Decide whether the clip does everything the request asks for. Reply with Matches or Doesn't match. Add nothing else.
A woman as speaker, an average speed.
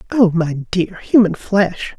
Matches